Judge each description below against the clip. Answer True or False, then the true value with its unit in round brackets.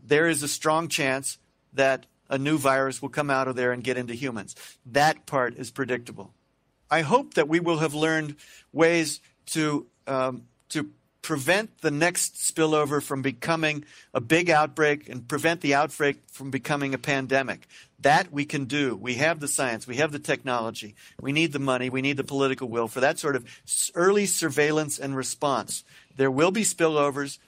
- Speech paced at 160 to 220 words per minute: True (180 wpm)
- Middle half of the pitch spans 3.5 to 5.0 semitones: False (2.9 semitones)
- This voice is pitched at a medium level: True (145 Hz)